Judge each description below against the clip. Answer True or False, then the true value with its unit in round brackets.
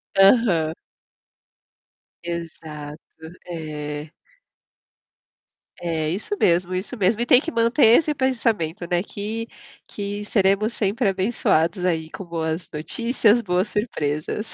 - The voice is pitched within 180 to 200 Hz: True (190 Hz)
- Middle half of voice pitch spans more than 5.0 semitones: True (5.4 semitones)